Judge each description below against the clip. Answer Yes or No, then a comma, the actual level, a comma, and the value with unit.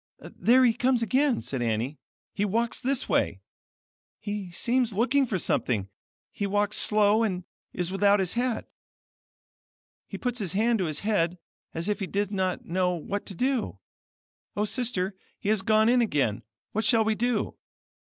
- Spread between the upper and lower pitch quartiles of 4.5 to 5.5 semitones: No, average, 4.1 semitones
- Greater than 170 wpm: No, average, 165 wpm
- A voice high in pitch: Yes, high, 210 Hz